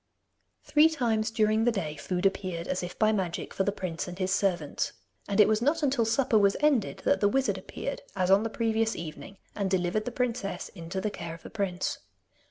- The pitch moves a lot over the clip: No, average, 3.6 semitones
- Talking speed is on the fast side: Yes, fast, 210 wpm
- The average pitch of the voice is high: Yes, high, 200 Hz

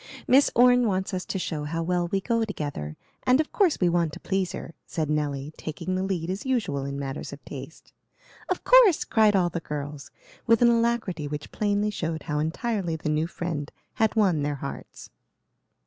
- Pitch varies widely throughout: Yes, wide, 6.3 semitones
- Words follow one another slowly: No, average, 195 wpm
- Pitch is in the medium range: Yes, medium, 175 Hz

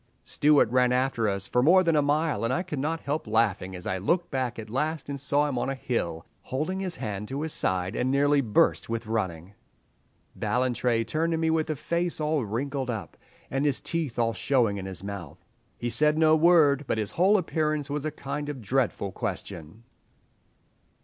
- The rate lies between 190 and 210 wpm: Yes, average, 200 wpm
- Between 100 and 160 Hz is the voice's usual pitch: Yes, low, 135 Hz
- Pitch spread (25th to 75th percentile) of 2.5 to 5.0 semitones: No, wide, 5.5 semitones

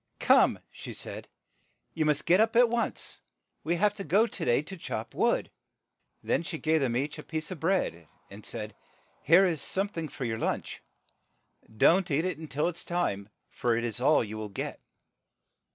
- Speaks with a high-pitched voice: No, medium, 155 Hz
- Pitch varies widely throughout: Yes, wide, 7.4 semitones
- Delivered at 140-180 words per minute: No, average, 190 wpm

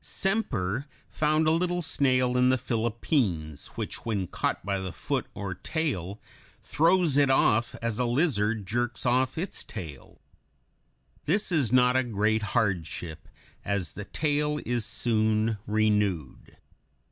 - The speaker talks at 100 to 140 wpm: Yes, slow, 135 wpm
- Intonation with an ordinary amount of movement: No, wide, 5.7 semitones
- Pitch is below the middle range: Yes, low, 120 Hz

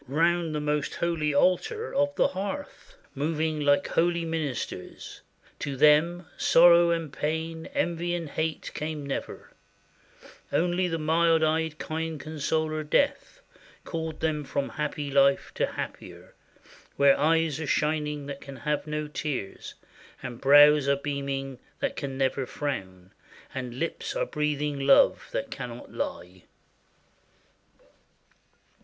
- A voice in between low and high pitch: Yes, medium, 150 Hz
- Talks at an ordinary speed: No, slow, 125 wpm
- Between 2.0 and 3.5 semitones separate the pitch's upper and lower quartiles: Yes, average, 2.7 semitones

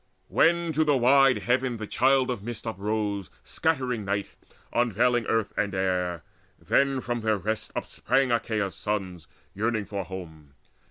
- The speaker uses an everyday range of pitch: Yes, average, 4.1 semitones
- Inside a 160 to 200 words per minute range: No, average, 140 wpm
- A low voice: Yes, low, 110 Hz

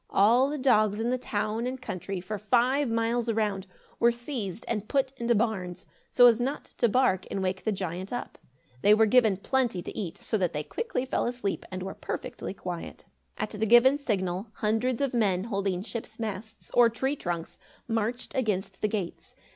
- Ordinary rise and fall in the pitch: Yes, average, 3.8 semitones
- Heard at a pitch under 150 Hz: No, high, 220 Hz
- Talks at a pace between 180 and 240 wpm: Yes, average, 185 wpm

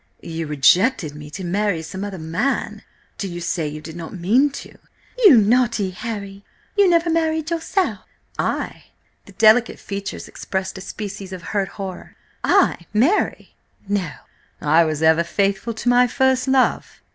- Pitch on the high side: Yes, high, 200 Hz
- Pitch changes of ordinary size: No, wide, 6.5 semitones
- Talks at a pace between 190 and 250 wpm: No, average, 155 wpm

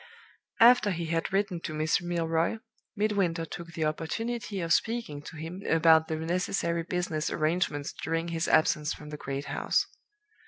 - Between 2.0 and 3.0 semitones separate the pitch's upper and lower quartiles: Yes, narrow, 2.4 semitones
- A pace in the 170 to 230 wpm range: No, average, 155 wpm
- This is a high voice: No, medium, 165 Hz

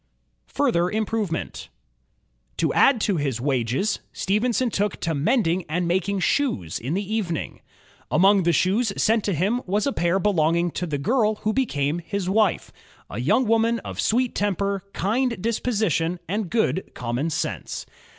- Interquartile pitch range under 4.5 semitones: No, average, 4.8 semitones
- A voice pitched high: Yes, high, 195 Hz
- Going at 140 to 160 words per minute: Yes, average, 150 wpm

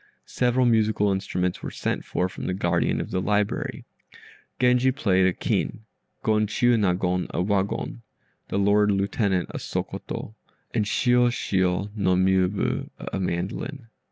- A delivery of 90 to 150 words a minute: Yes, slow, 135 wpm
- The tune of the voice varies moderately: Yes, average, 3.0 semitones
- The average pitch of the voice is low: Yes, low, 100 Hz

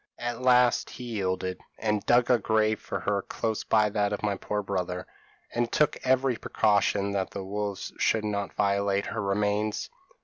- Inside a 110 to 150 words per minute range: No, average, 170 wpm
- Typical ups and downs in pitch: No, narrow, 2.1 semitones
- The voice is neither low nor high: No, low, 105 Hz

